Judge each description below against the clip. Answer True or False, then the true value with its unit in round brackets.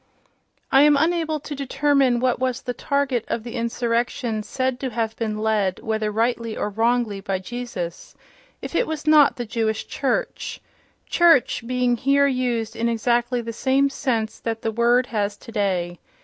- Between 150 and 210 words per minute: True (160 wpm)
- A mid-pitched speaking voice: False (240 Hz)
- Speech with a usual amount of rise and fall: True (3.2 semitones)